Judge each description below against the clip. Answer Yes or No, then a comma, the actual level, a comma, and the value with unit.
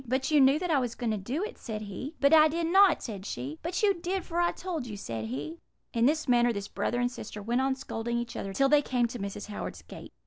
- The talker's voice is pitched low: No, very high, 250 Hz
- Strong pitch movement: Yes, wide, 6.7 semitones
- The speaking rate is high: Yes, fast, 270 wpm